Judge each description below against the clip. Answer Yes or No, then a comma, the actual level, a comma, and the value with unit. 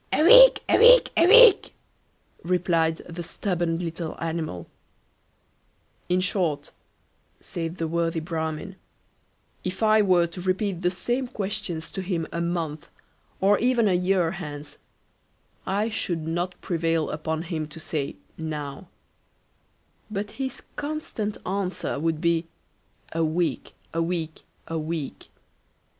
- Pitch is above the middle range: No, medium, 175 Hz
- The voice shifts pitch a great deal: No, average, 3.3 semitones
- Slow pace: Yes, slow, 125 wpm